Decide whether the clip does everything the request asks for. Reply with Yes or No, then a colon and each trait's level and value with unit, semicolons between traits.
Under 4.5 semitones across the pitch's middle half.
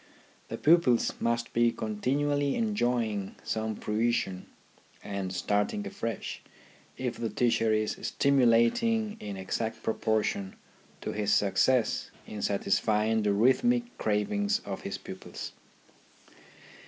No: average, 4.8 semitones